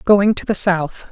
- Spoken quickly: Yes, fast, 215 wpm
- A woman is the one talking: Yes, female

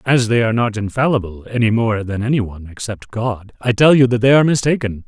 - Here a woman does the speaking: No, male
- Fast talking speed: Yes, fast, 225 wpm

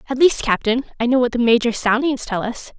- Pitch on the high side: Yes, high, 245 Hz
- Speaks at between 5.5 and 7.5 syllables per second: Yes, 5.8 syllables/s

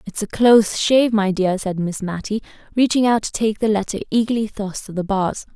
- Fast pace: Yes, fast, 215 wpm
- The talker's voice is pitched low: No, high, 210 Hz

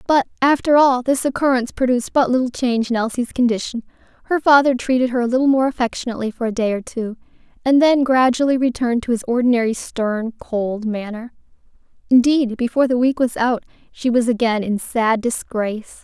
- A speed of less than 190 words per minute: Yes, average, 175 wpm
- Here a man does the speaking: No, female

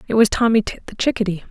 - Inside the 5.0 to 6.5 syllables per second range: No, 7.1 syllables/s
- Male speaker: No, female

